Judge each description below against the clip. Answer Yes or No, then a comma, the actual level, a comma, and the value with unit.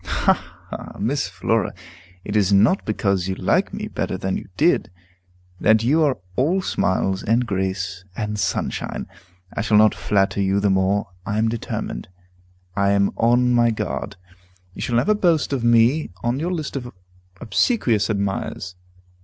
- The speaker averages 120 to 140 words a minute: No, average, 160 wpm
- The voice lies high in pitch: No, low, 110 Hz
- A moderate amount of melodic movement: Yes, average, 4.0 semitones